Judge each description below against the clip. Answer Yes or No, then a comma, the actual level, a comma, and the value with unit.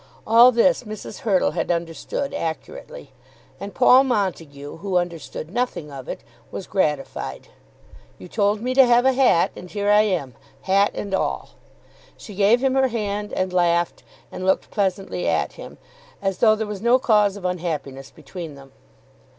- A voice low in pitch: No, high, 200 Hz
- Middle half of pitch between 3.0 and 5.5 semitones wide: Yes, average, 5.2 semitones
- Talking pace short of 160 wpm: No, average, 165 wpm